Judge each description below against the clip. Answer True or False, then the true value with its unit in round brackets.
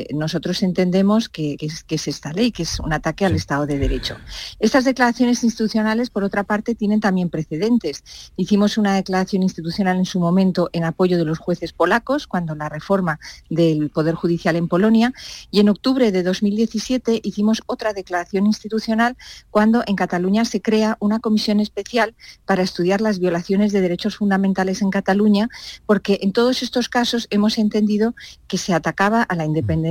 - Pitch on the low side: False (200 Hz)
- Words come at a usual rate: True (175 wpm)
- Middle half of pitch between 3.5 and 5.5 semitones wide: True (3.8 semitones)